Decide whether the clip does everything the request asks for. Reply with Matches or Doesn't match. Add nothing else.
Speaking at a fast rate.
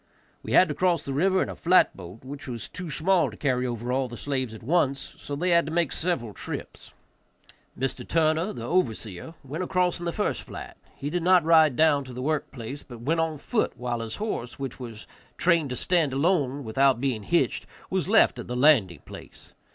Matches